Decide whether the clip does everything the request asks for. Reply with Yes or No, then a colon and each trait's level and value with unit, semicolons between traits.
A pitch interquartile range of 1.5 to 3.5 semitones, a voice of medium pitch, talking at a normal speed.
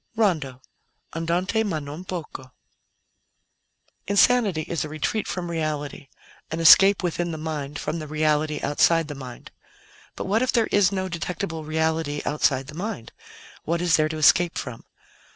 Yes: average, 3.2 semitones; medium, 160 Hz; average, 150 wpm